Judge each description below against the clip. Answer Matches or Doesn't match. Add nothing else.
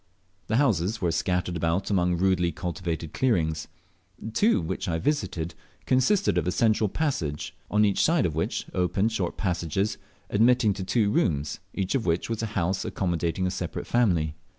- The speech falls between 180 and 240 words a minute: Doesn't match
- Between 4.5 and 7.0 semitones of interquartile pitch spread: Matches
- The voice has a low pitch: Matches